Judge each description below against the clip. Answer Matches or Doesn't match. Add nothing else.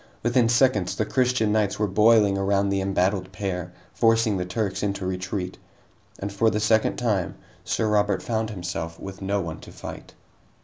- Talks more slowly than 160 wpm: Doesn't match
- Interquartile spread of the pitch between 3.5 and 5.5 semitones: Doesn't match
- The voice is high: Doesn't match